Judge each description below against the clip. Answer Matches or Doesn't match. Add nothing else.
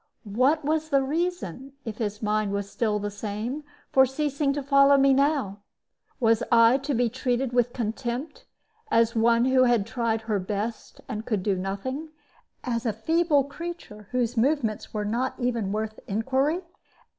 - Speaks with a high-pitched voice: Matches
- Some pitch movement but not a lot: Matches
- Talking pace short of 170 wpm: Matches